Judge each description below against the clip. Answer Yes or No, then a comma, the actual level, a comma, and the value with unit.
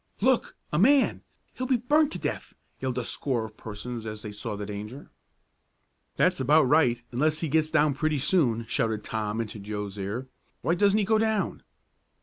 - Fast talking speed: No, average, 180 wpm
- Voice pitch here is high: No, low, 130 Hz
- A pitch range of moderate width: No, wide, 7.6 semitones